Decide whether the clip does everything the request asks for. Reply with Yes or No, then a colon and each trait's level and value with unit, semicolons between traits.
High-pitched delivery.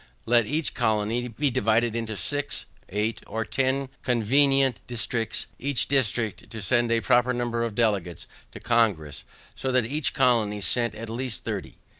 No: low, 115 Hz